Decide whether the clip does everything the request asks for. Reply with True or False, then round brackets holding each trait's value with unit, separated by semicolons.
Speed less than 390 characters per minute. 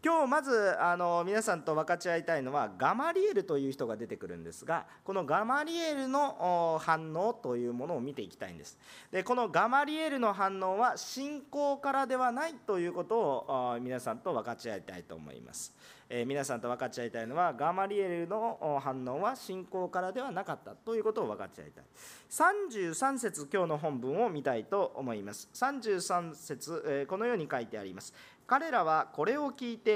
True (375 characters per minute)